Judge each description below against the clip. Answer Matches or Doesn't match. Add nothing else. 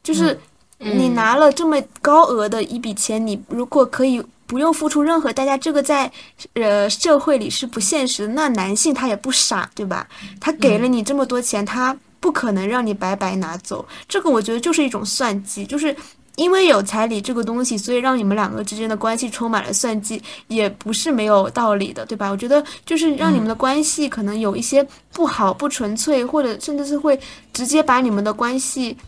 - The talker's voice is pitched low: Doesn't match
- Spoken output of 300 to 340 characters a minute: Matches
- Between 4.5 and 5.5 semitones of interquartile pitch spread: Matches